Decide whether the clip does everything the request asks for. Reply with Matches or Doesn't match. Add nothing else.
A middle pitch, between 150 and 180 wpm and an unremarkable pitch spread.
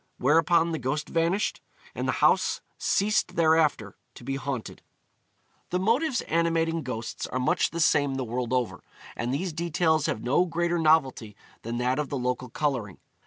Matches